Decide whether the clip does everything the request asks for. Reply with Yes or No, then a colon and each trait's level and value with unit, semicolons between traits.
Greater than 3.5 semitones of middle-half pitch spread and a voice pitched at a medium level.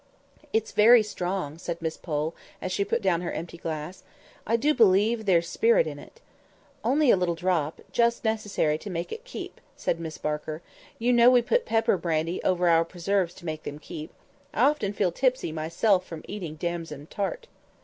Yes: average, 5.3 semitones; medium, 180 Hz